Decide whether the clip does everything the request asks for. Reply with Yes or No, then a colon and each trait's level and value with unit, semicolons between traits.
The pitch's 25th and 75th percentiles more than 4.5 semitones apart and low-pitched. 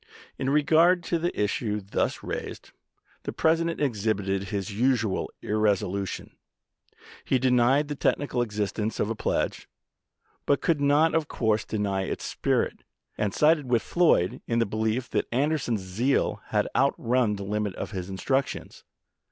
Yes: wide, 5.6 semitones; low, 115 Hz